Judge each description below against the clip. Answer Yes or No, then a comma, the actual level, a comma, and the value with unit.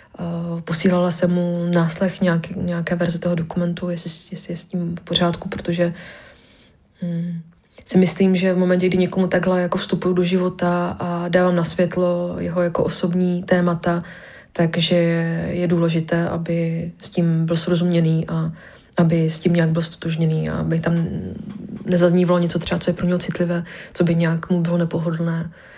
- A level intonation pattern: Yes, narrow, 1.1 semitones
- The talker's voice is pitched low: No, medium, 175 Hz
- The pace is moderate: Yes, average, 160 wpm